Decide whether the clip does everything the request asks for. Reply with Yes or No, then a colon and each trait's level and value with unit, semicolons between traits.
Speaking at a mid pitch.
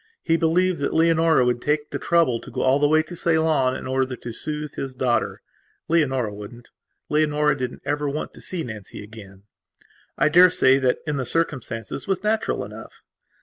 Yes: medium, 145 Hz